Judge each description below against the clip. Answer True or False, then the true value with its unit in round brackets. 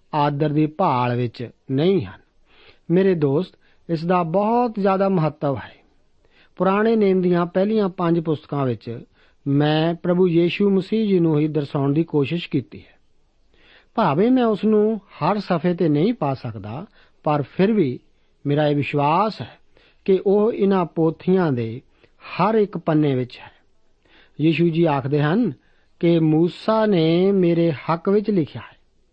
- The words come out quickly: False (145 wpm)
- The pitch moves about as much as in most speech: True (4.8 semitones)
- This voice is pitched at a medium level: True (170 Hz)